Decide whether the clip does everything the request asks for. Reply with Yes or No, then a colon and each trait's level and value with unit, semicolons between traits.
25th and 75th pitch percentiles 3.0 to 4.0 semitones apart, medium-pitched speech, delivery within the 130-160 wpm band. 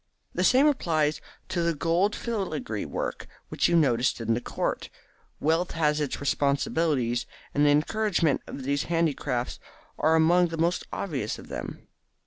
Yes: average, 3.6 semitones; medium, 155 Hz; average, 150 wpm